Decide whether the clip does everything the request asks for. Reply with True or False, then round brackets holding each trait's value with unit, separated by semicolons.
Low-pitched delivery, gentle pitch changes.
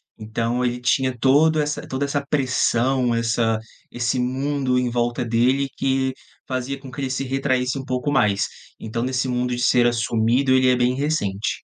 True (125 Hz; 2.0 semitones)